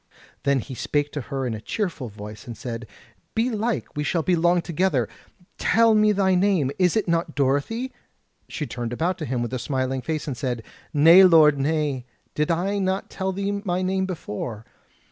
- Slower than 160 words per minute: No, average, 185 wpm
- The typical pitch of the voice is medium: Yes, medium, 160 Hz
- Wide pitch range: Yes, wide, 6.4 semitones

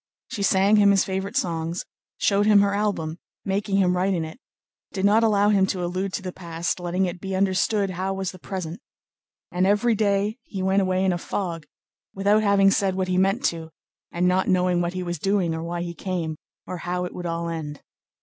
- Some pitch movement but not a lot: No, narrow, 2.2 semitones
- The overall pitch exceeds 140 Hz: Yes, high, 190 Hz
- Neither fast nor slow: No, fast, 215 wpm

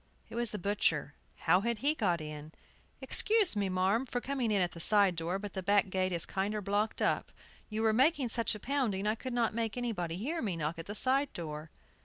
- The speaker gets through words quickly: Yes, fast, 225 wpm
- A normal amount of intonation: Yes, average, 4.5 semitones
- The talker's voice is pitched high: Yes, high, 205 Hz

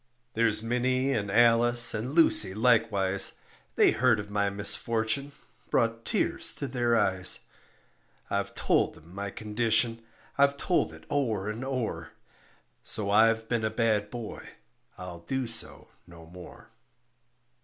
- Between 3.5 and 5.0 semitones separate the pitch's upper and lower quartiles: No, average, 2.9 semitones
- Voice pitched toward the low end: Yes, low, 115 Hz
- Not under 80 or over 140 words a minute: Yes, slow, 135 wpm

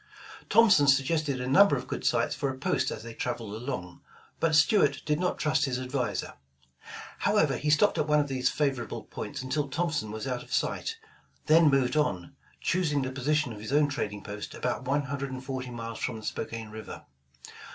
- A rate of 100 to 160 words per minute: No, average, 195 wpm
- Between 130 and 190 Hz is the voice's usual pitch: Yes, low, 135 Hz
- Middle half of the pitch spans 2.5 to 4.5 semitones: Yes, average, 3.6 semitones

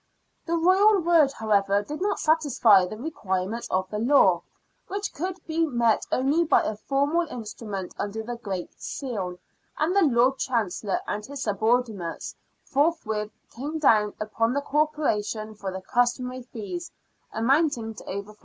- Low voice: No, high, 240 Hz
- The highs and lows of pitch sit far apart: Yes, wide, 6.3 semitones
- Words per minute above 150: No, average, 145 wpm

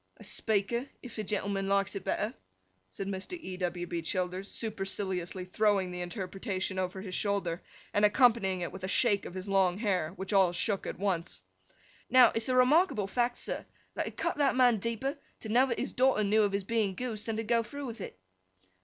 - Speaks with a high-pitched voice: Yes, high, 200 Hz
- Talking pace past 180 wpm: Yes, average, 200 wpm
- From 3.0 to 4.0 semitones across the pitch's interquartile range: Yes, average, 3.7 semitones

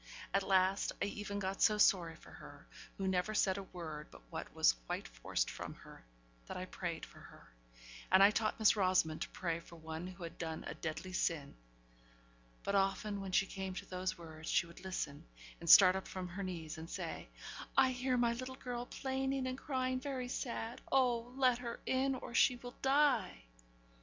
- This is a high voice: Yes, high, 195 Hz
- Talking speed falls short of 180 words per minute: No, average, 195 wpm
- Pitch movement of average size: No, wide, 6.2 semitones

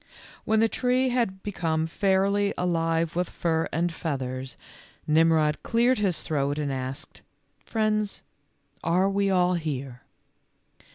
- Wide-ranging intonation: No, average, 4.5 semitones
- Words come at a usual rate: No, slow, 120 wpm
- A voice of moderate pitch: Yes, medium, 170 Hz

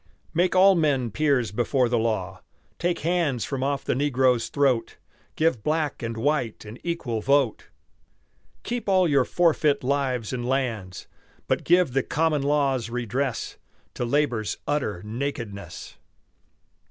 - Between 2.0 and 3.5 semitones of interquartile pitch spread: No, average, 4.4 semitones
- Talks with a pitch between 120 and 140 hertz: Yes, low, 135 Hz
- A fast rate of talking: No, slow, 135 wpm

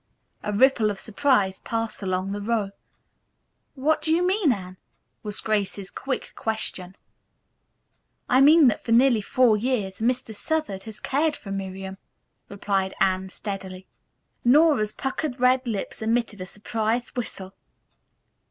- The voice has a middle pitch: No, high, 220 Hz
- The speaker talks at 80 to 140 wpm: Yes, slow, 135 wpm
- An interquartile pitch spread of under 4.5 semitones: No, average, 4.8 semitones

